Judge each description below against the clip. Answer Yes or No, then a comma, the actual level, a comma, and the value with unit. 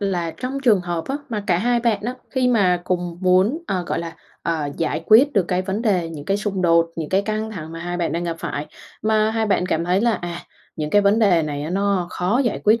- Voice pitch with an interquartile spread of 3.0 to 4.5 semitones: Yes, average, 4.2 semitones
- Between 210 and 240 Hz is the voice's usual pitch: No, medium, 185 Hz